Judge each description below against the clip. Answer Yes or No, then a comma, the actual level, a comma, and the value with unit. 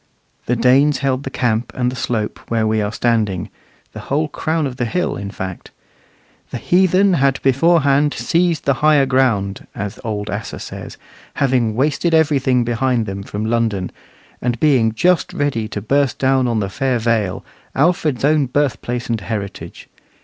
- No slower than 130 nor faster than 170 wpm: Yes, average, 165 wpm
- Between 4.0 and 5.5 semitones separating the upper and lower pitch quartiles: Yes, average, 4.5 semitones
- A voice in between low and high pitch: No, low, 125 Hz